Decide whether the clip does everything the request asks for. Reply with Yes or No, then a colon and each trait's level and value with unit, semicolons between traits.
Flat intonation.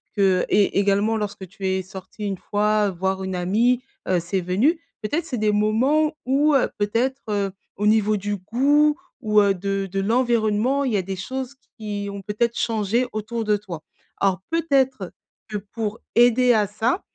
No: average, 3.7 semitones